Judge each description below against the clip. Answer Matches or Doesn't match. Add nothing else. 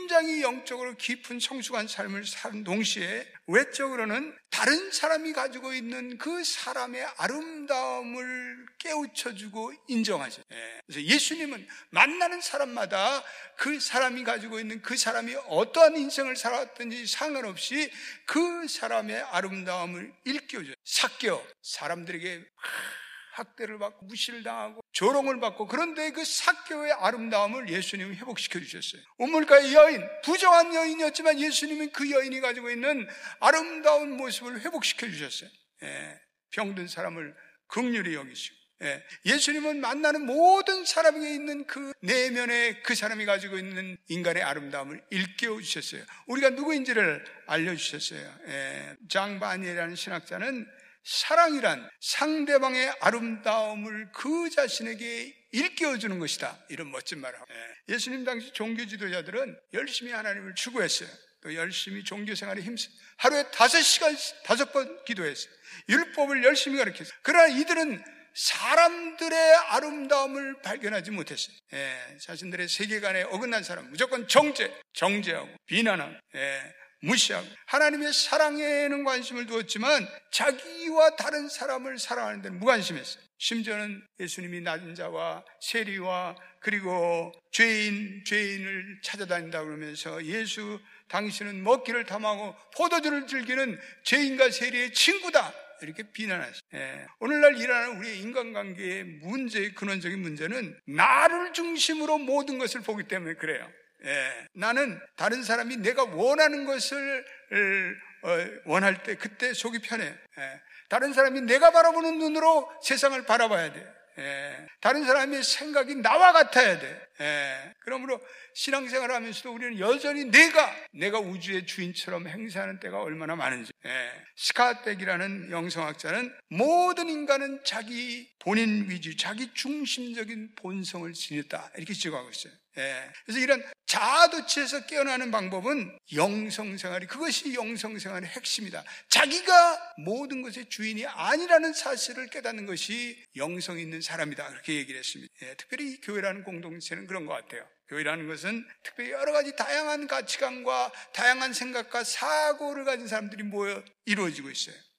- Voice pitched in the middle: Doesn't match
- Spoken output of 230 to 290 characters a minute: Doesn't match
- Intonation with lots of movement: Matches